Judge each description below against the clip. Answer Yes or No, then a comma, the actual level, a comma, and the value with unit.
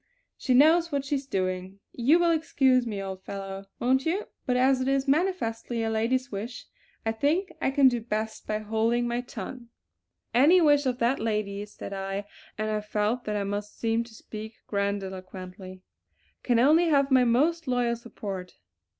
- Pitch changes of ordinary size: Yes, average, 4.6 semitones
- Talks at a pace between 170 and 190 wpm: Yes, average, 175 wpm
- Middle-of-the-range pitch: No, high, 235 Hz